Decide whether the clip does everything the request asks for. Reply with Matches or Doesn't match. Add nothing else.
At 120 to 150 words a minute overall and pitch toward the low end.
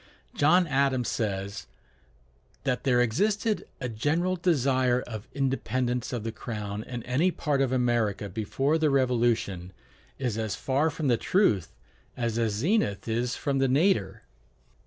Matches